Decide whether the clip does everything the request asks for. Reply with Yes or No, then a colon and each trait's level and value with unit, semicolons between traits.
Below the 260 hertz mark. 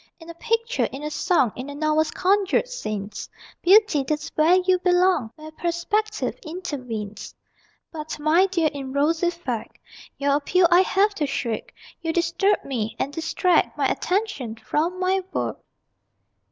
No: very high, 325 Hz